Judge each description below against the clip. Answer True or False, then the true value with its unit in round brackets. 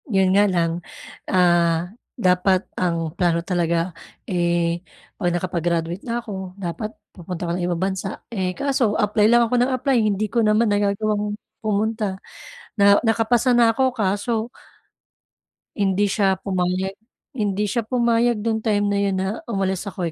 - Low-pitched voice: False (200 Hz)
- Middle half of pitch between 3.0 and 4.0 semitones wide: True (3.4 semitones)